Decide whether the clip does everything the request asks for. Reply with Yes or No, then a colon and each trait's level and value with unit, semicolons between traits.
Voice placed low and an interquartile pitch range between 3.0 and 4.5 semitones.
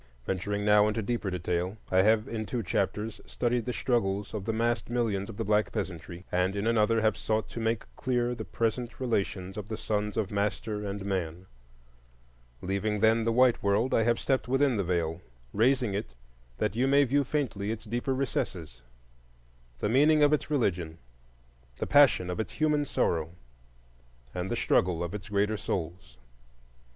Yes: low, 105 Hz; average, 4.1 semitones